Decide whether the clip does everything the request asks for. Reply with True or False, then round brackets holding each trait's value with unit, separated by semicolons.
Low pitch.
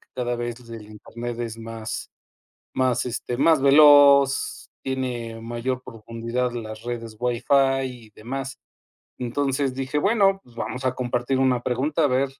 True (125 Hz)